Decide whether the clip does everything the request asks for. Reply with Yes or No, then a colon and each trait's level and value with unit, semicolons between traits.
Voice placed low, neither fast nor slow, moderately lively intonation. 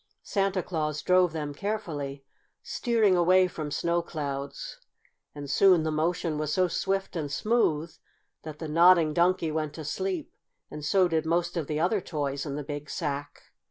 No: medium, 160 Hz; average, 165 wpm; average, 3.5 semitones